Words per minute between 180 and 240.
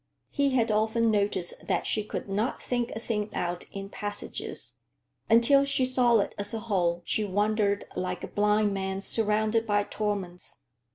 No: average, 165 wpm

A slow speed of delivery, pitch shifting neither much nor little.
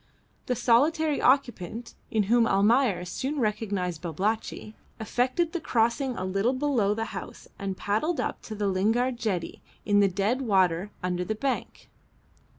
No: average, 150 wpm; average, 4.4 semitones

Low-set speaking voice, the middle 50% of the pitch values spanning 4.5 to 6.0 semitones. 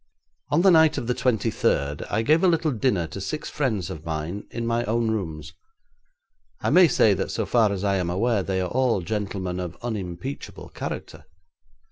Yes: low, 105 Hz; wide, 5.4 semitones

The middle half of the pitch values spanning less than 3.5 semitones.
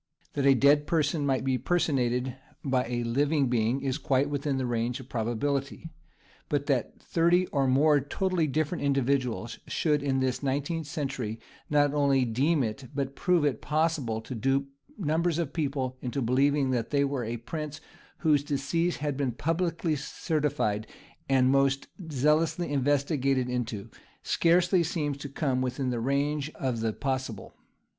Yes: narrow, 2.6 semitones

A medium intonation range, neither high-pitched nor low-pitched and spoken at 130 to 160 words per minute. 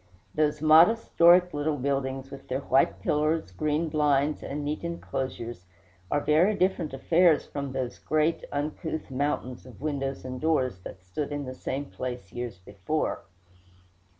Yes: average, 3.0 semitones; medium, 145 Hz; average, 150 wpm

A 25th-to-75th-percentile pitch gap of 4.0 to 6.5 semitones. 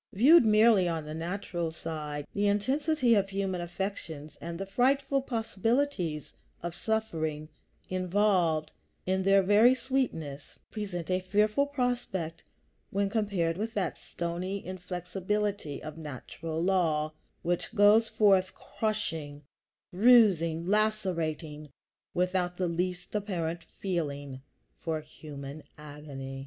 Yes: average, 4.6 semitones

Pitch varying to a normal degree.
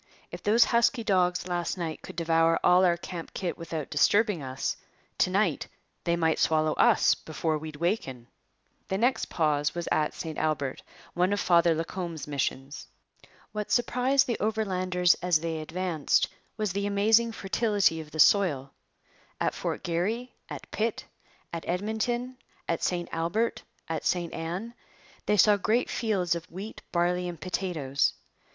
Yes: average, 4.3 semitones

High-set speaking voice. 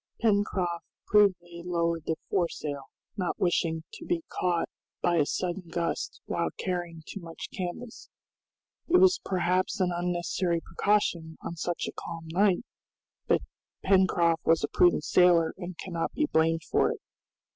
No: medium, 175 Hz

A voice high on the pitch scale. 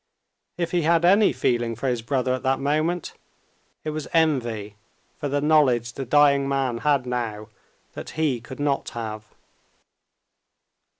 No: low, 135 Hz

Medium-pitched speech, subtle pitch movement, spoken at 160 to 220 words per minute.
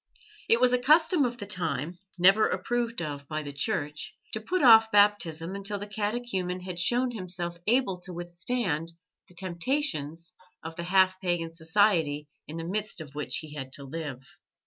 No: medium, 180 Hz; average, 5.1 semitones; average, 170 wpm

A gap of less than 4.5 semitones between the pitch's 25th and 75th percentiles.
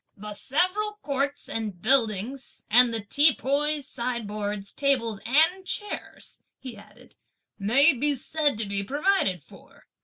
No: wide, 5.6 semitones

